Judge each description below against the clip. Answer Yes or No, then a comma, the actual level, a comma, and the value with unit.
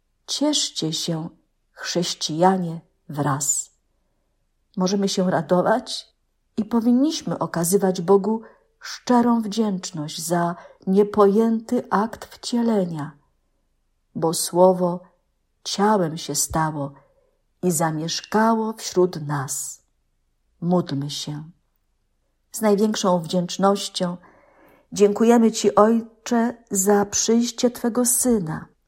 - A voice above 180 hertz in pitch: Yes, high, 190 Hz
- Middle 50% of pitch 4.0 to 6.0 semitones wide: Yes, average, 5.2 semitones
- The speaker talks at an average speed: No, slow, 80 wpm